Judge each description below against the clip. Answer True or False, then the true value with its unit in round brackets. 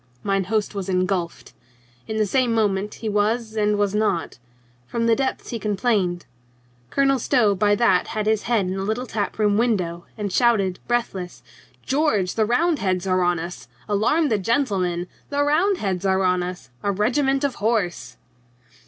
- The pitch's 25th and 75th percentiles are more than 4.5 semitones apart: False (4.0 semitones)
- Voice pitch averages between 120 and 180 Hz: False (210 Hz)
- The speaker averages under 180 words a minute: True (170 wpm)